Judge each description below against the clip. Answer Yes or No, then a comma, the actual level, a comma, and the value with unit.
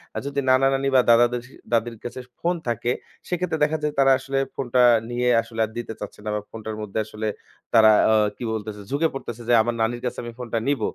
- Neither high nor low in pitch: No, low, 120 Hz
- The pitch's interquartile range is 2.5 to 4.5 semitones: Yes, average, 3.3 semitones